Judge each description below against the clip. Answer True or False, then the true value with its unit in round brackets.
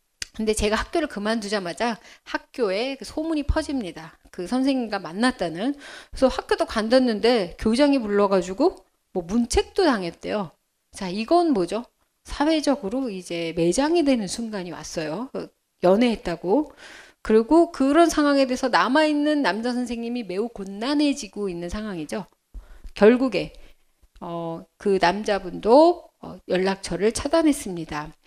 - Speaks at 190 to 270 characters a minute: False (295 characters per minute)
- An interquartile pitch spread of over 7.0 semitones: True (7.4 semitones)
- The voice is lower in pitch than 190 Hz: False (225 Hz)